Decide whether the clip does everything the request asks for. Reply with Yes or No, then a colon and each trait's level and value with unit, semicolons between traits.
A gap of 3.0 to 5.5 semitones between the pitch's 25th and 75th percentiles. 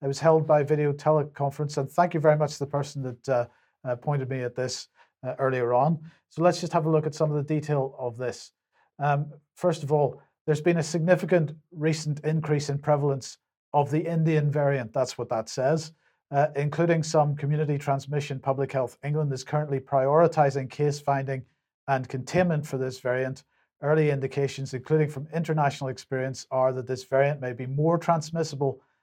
No: narrow, 2.5 semitones